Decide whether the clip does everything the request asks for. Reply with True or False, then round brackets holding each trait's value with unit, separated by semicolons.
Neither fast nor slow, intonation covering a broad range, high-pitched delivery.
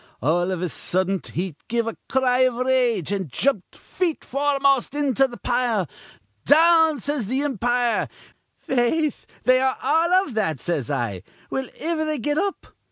True (160 wpm; 6.4 semitones; 255 Hz)